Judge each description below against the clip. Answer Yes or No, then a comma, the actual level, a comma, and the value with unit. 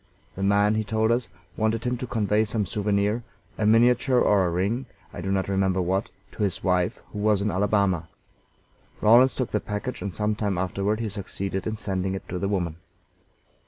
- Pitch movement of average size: No, narrow, 2.2 semitones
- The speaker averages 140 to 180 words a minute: No, average, 195 wpm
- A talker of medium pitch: No, low, 105 Hz